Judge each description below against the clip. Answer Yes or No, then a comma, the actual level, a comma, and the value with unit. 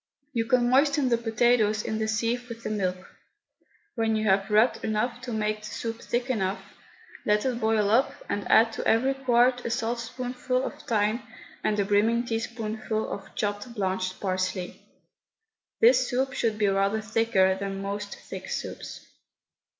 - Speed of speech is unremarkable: Yes, average, 160 wpm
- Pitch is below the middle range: No, high, 225 Hz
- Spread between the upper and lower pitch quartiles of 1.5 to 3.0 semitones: Yes, average, 2.7 semitones